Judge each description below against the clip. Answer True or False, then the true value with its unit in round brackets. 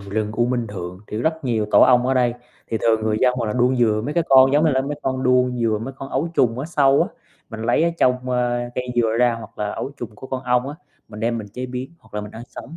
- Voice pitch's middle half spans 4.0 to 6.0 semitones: False (2.9 semitones)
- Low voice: True (125 Hz)